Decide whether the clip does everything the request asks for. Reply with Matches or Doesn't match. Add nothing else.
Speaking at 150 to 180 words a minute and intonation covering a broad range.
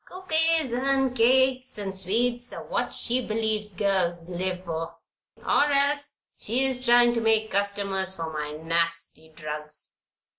Doesn't match